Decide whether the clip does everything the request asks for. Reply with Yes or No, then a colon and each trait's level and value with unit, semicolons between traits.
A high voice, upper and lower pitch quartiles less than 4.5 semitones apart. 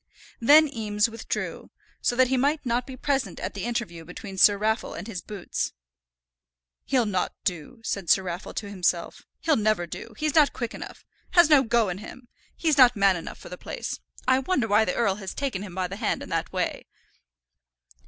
No: high, 220 Hz; average, 5.0 semitones